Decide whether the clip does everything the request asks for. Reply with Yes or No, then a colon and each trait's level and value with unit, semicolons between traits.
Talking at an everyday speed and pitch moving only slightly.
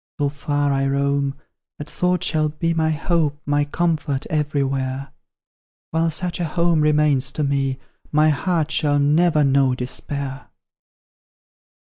No: slow, 130 wpm; narrow, 2.2 semitones